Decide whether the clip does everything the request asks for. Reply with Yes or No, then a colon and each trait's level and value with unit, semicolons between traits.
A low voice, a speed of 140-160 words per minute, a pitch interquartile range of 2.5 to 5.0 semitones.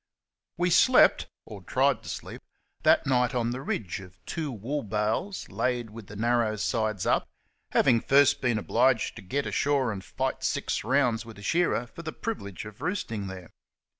No: low, 120 Hz; average, 175 wpm; average, 4.7 semitones